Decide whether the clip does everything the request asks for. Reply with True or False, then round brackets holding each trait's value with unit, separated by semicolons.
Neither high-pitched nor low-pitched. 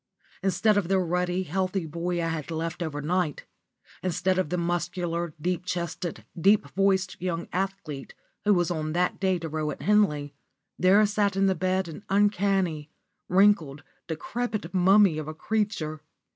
True (180 Hz)